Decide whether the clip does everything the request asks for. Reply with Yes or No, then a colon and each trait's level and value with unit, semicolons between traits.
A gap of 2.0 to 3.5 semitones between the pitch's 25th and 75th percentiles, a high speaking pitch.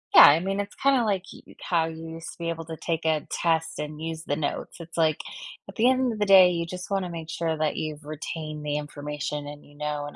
No: average, 2.8 semitones; medium, 160 Hz